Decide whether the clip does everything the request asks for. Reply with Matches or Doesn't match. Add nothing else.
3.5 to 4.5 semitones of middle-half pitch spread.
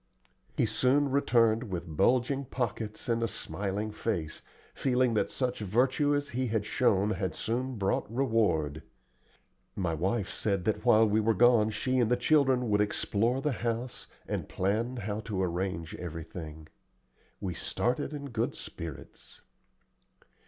Matches